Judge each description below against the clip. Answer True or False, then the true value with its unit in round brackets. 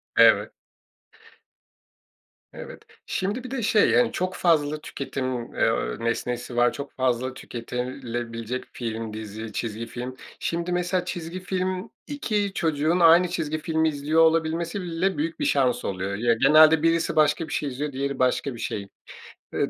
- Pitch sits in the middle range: True (150 Hz)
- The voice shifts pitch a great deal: True (5.8 semitones)